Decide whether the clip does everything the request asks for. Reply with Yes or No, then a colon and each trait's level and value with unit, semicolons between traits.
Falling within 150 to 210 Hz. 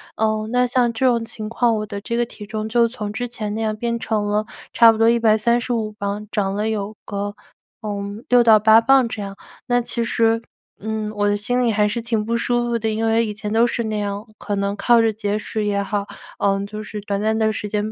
No: high, 220 Hz